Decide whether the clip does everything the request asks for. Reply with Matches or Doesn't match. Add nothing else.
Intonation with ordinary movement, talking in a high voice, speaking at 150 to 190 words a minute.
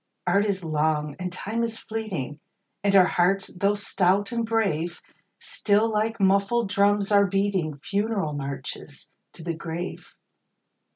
Doesn't match